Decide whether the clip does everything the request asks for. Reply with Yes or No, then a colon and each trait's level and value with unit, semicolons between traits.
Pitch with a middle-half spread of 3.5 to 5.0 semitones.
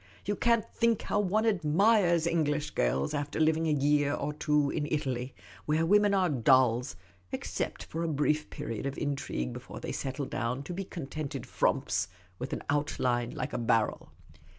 Yes: average, 4.1 semitones